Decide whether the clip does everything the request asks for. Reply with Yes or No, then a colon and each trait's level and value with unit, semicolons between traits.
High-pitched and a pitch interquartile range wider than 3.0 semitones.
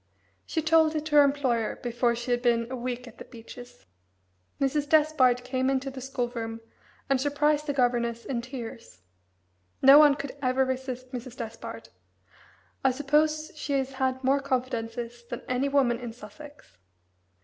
No: very high, 255 Hz; average, 2.7 semitones